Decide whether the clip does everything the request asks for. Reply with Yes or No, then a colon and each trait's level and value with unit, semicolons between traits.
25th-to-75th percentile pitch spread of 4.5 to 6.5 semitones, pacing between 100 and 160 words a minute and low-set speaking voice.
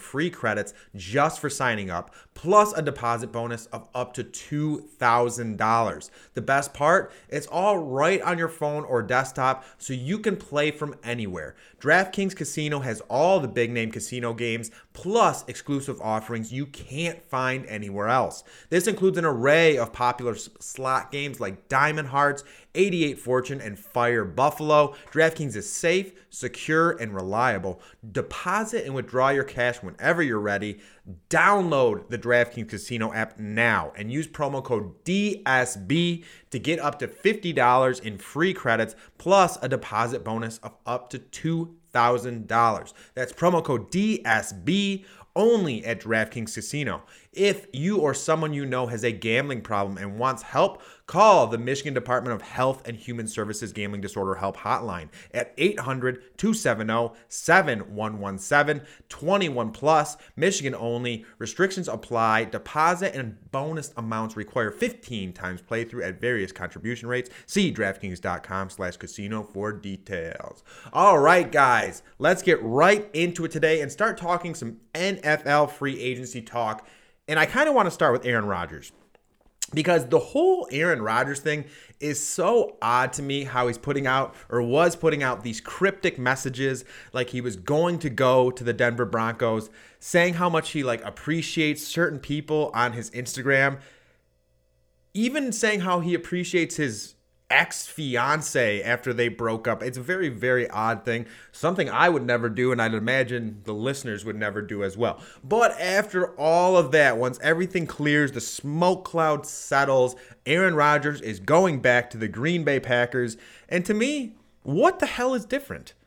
Yes: wide, 5.4 semitones; average, 150 wpm; low, 130 Hz